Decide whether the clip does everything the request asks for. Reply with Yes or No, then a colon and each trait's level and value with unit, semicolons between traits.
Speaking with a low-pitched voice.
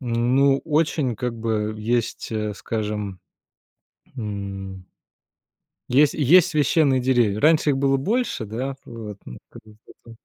Yes: low, 120 Hz